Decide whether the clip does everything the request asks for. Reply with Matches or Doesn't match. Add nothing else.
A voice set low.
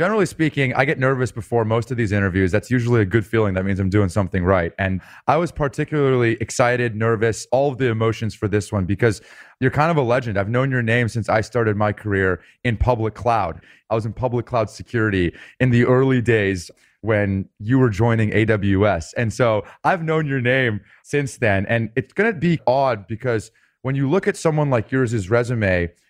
Matches